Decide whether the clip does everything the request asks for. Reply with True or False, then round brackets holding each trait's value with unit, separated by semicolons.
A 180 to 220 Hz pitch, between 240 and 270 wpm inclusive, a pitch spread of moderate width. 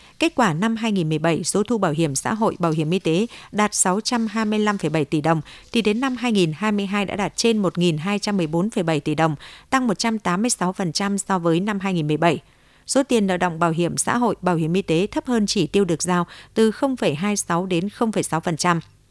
False (190 Hz; 175 wpm; 4.4 semitones)